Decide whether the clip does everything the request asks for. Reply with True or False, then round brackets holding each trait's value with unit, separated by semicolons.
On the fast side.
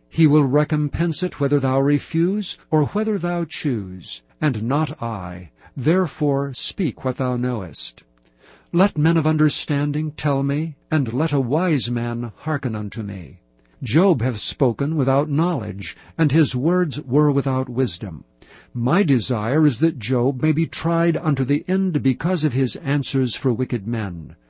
False (150 wpm)